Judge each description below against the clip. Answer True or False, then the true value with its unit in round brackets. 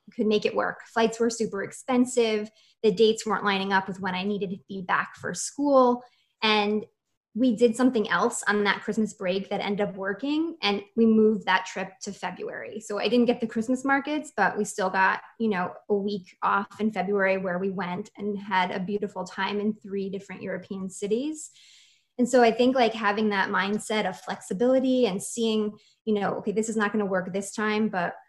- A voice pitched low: False (210 Hz)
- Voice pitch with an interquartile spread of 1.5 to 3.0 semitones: True (2.6 semitones)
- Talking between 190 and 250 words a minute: True (205 wpm)